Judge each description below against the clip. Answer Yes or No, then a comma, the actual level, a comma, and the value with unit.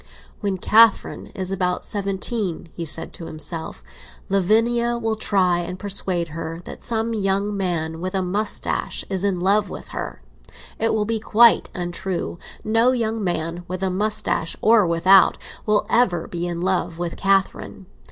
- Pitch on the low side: No, high, 190 Hz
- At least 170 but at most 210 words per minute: No, average, 155 wpm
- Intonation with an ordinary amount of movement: Yes, average, 3.5 semitones